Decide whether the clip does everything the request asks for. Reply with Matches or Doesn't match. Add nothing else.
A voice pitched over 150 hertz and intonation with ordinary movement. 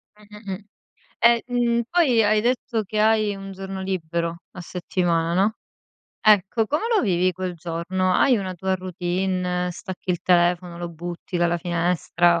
Matches